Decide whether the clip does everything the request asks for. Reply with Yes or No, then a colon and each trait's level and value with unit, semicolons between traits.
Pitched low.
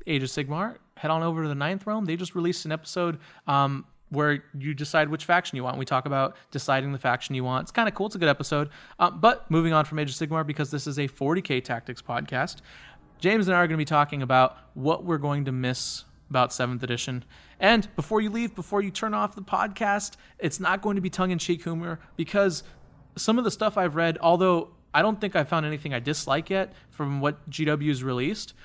No: medium, 155 Hz